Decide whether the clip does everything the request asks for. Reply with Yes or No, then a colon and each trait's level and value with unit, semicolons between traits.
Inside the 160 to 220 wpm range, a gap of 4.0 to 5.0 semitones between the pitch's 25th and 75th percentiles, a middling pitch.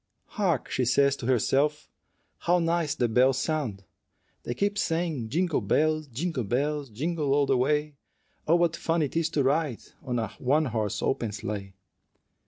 Yes: average, 165 wpm; average, 4.7 semitones; medium, 145 Hz